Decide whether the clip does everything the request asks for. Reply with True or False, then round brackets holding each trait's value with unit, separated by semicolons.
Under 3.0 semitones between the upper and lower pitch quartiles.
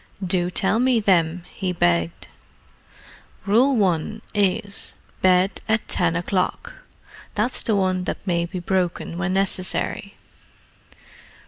True (2.6 semitones)